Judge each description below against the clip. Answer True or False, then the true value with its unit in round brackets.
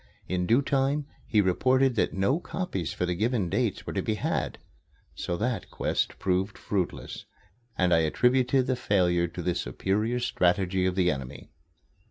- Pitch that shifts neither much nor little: False (5.7 semitones)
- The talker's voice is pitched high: False (95 Hz)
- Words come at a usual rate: True (165 wpm)